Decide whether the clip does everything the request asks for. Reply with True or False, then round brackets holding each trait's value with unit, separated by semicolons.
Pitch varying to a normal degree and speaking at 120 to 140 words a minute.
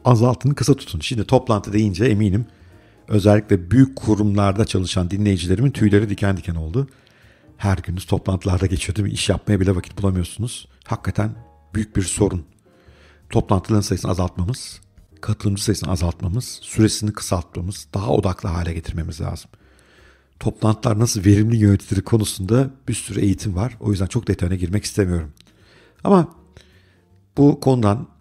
True (3.1 semitones; 130 wpm)